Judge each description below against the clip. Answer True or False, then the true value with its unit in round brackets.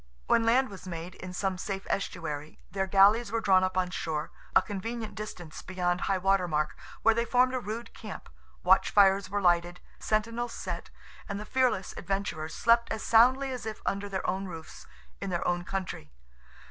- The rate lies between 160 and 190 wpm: True (180 wpm)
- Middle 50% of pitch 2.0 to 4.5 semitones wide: True (3.7 semitones)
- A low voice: False (195 Hz)